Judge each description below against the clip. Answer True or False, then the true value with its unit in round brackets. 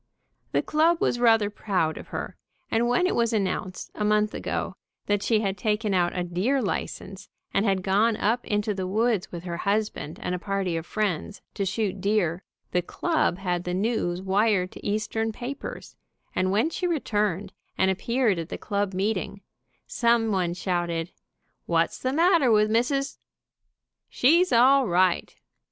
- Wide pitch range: False (3.8 semitones)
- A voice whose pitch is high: True (205 Hz)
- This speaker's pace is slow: False (165 wpm)